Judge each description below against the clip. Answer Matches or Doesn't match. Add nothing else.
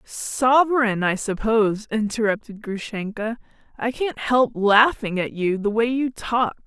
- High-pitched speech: Matches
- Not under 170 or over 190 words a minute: Doesn't match